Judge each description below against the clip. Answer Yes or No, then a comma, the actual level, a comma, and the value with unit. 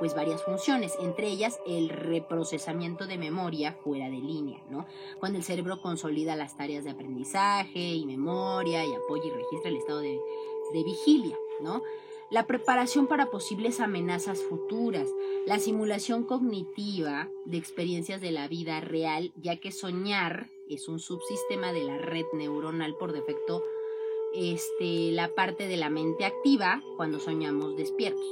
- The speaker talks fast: No, average, 150 wpm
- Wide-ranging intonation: Yes, wide, 6.4 semitones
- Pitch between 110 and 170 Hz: No, medium, 185 Hz